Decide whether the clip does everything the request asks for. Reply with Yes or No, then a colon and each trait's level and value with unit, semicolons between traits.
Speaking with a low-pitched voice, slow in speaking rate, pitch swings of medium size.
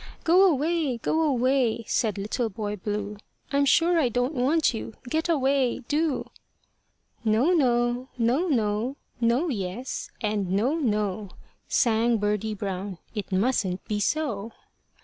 No: high, 240 Hz; slow, 130 wpm; average, 5.0 semitones